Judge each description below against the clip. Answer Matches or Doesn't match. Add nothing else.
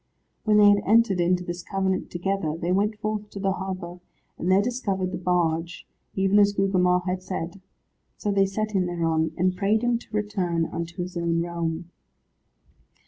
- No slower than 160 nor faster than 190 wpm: Matches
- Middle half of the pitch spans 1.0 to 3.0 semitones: Matches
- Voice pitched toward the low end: Doesn't match